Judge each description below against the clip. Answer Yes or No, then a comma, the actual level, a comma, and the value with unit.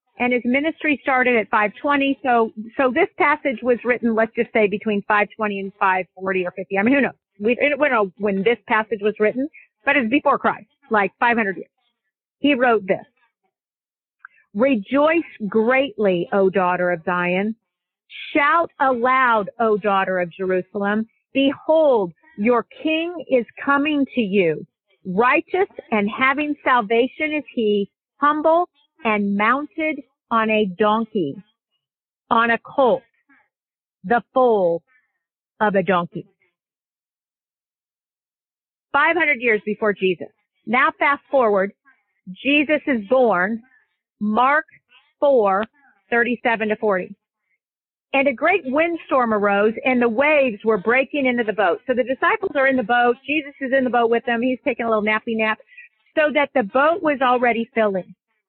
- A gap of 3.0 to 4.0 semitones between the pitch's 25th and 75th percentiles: No, average, 5.0 semitones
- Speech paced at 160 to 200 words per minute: No, average, 145 wpm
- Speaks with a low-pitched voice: No, high, 235 Hz